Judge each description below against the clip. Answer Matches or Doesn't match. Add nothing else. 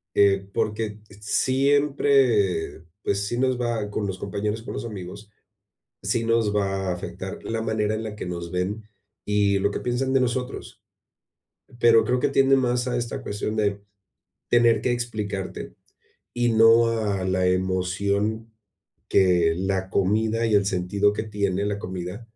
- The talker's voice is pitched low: Matches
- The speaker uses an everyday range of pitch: Matches